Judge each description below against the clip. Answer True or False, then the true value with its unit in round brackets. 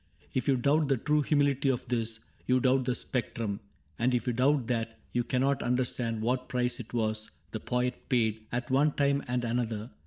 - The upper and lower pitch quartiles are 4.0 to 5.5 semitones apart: False (2.5 semitones)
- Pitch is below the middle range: True (125 Hz)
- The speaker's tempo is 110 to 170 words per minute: False (190 wpm)